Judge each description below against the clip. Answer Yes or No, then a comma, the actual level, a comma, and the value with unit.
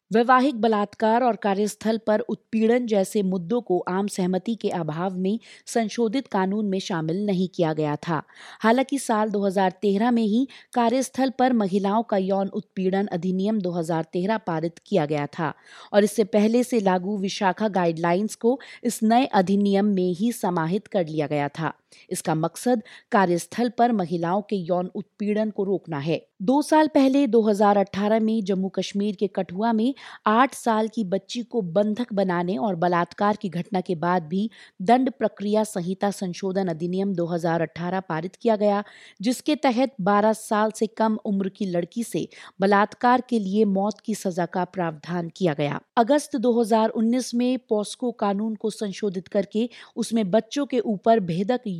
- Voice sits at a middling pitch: No, high, 205 Hz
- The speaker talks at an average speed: Yes, average, 155 wpm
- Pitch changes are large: No, average, 3.5 semitones